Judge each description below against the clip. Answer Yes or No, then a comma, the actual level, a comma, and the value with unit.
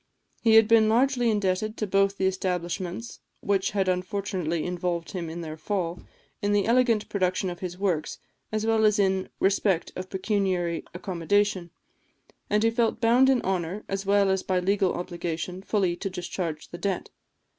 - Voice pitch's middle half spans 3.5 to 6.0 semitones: No, average, 2.8 semitones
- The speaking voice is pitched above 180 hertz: Yes, high, 190 Hz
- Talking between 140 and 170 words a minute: Yes, average, 165 wpm